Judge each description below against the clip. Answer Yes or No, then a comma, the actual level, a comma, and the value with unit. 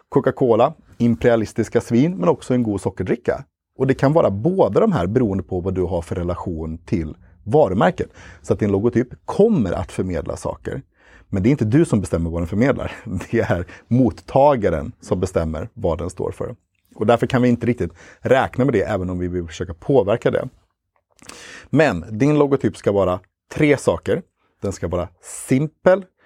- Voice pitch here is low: Yes, low, 110 Hz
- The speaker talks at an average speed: Yes, average, 180 wpm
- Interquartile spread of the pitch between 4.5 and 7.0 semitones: Yes, wide, 5.5 semitones